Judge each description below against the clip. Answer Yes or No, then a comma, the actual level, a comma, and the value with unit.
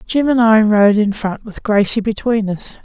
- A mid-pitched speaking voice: No, high, 215 Hz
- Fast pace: Yes, fast, 210 wpm